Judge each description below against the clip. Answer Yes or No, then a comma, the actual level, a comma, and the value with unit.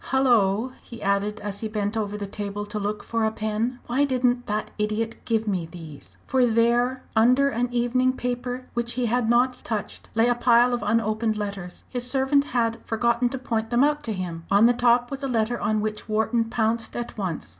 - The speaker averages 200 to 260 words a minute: Yes, fast, 205 wpm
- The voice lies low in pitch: No, high, 230 Hz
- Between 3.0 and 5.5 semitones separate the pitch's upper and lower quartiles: No, narrow, 2.6 semitones